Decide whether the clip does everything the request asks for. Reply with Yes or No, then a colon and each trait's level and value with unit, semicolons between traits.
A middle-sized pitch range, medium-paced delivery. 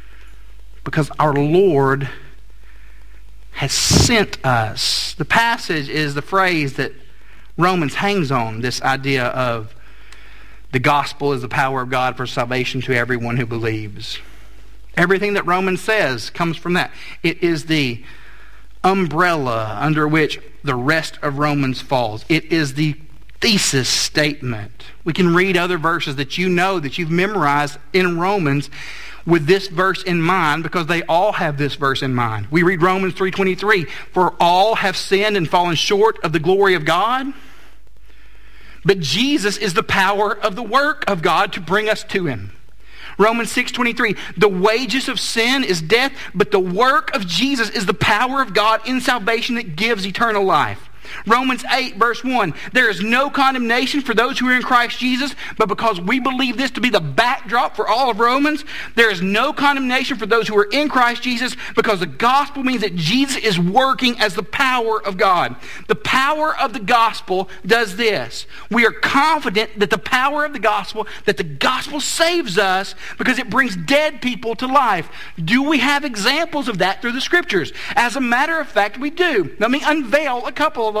No: wide, 8.1 semitones; average, 175 wpm